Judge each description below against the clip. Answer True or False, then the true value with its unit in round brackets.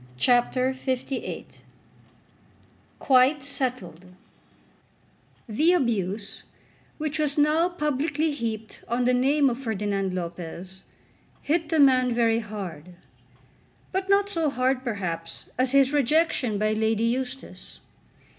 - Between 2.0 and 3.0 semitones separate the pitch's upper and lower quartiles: False (5.3 semitones)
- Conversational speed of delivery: False (110 wpm)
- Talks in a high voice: True (255 Hz)